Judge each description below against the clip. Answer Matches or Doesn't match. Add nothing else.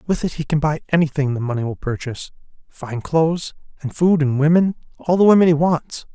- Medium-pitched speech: Matches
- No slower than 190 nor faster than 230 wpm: Matches